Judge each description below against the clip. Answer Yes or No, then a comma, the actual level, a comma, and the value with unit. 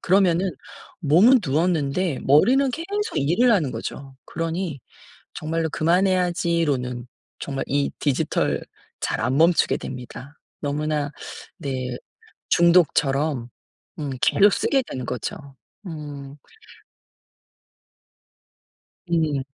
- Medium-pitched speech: Yes, medium, 155 Hz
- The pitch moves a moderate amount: Yes, average, 4.3 semitones